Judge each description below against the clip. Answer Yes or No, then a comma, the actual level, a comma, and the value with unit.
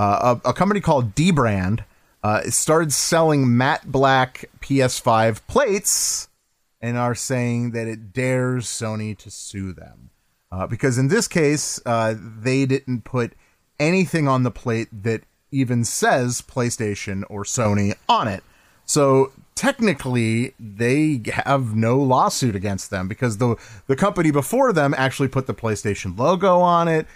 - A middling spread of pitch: Yes, average, 4.2 semitones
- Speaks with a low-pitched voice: Yes, low, 125 Hz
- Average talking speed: Yes, average, 145 wpm